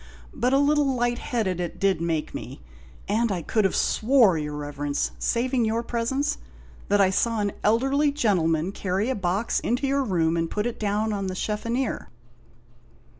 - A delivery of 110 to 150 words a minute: No, average, 175 wpm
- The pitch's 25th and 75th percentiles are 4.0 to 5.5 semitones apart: Yes, average, 4.7 semitones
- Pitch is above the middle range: Yes, high, 215 Hz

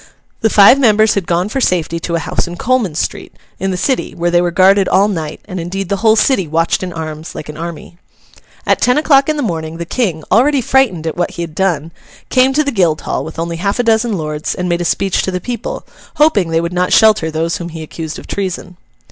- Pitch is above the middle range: No, medium, 180 Hz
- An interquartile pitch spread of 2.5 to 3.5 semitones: No, average, 4.8 semitones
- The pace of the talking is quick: Yes, fast, 240 wpm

